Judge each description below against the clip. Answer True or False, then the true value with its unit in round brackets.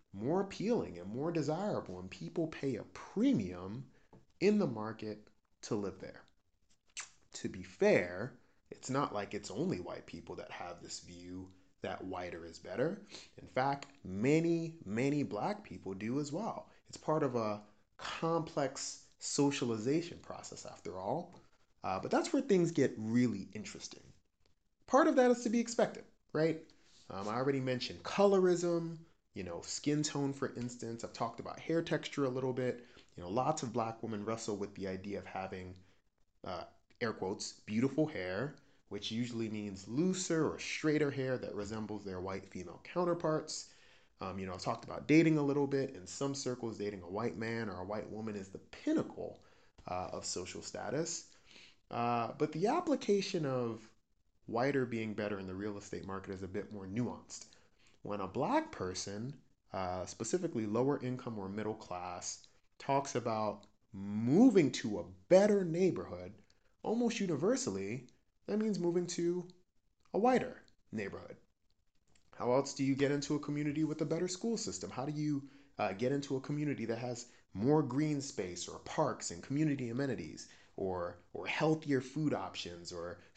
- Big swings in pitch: True (7.0 semitones)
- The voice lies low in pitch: True (125 Hz)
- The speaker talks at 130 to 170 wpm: True (165 wpm)